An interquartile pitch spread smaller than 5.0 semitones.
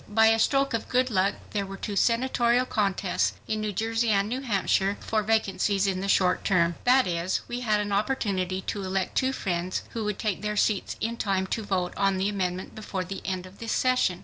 Yes: average, 3.0 semitones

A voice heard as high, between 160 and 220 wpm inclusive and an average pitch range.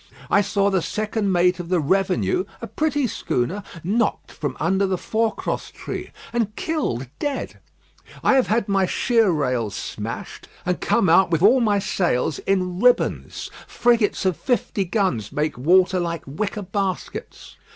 No: high, 195 Hz; average, 150 wpm; average, 4.1 semitones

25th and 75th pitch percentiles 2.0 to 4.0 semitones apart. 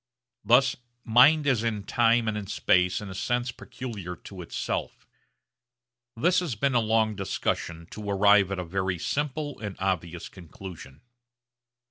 No: average, 4.5 semitones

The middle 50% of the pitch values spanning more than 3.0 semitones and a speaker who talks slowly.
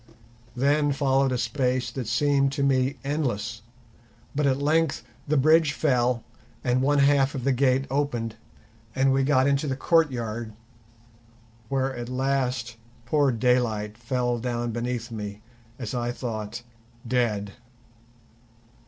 No: average, 2.7 semitones; slow, 130 wpm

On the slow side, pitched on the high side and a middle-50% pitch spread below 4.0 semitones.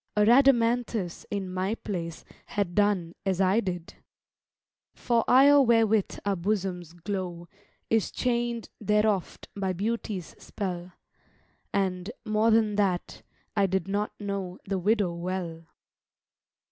Yes: slow, 120 wpm; high, 200 Hz; average, 3.2 semitones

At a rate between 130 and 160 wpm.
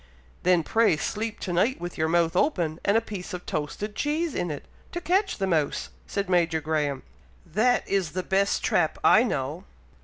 No: average, 185 wpm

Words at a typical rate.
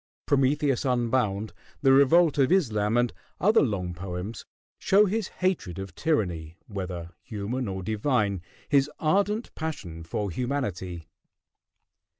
No: slow, 120 wpm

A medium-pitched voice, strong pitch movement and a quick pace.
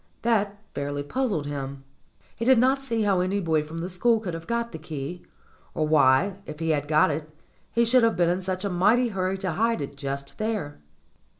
Yes: medium, 180 Hz; wide, 6.8 semitones; fast, 210 wpm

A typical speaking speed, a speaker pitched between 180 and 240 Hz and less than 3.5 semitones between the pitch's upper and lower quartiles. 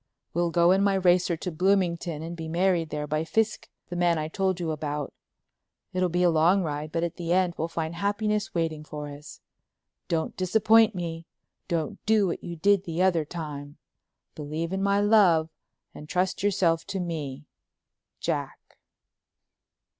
No: average, 160 wpm; medium, 170 Hz; average, 3.0 semitones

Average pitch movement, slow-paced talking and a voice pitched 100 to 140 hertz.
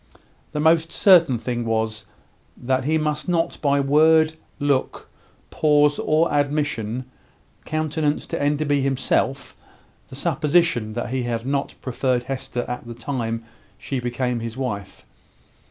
Yes: average, 3.9 semitones; slow, 130 wpm; low, 135 Hz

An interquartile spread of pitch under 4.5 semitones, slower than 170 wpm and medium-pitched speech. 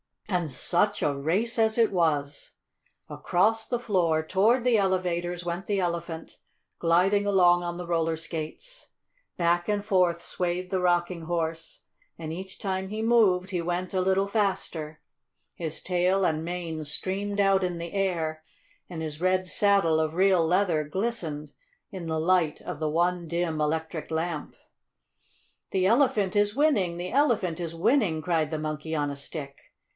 Yes: average, 3.2 semitones; average, 160 wpm; medium, 175 Hz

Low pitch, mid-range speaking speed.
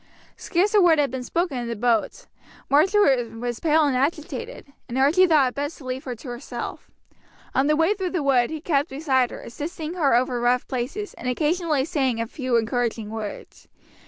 No: very high, 275 Hz; average, 195 wpm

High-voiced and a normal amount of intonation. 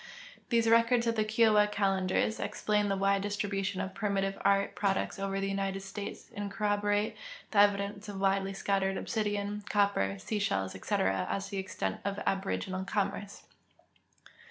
No: high, 200 Hz; narrow, 1.1 semitones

